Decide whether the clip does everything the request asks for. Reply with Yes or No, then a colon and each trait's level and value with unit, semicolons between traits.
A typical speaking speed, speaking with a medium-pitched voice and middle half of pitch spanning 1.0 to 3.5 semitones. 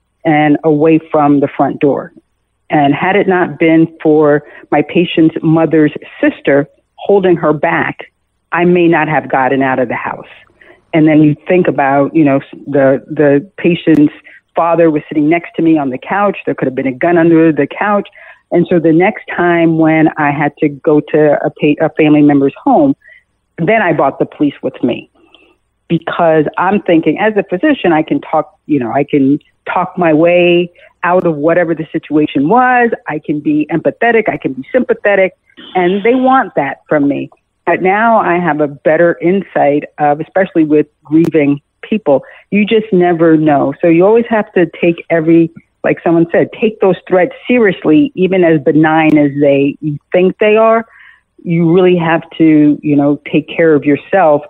Yes: average, 180 wpm; medium, 165 Hz; average, 3.2 semitones